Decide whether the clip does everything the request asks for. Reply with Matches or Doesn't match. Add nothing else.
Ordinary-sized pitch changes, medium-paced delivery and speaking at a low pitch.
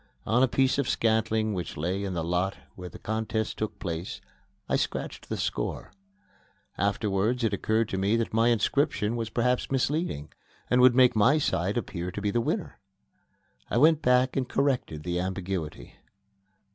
Matches